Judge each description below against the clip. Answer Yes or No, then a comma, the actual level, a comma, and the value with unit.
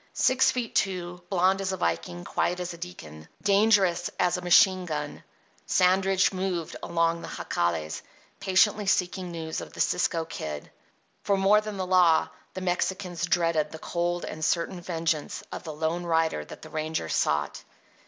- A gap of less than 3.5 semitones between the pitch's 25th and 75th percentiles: Yes, average, 2.8 semitones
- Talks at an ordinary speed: Yes, average, 165 wpm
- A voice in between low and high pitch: Yes, medium, 175 Hz